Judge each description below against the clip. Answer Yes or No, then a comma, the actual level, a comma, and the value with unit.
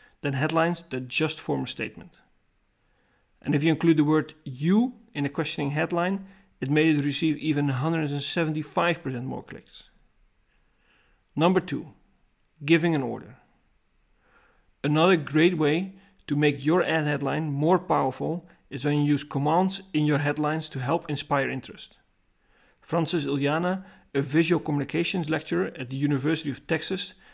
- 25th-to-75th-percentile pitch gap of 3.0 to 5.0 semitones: No, narrow, 2.6 semitones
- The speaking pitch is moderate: Yes, medium, 155 Hz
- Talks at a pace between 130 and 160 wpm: Yes, average, 140 wpm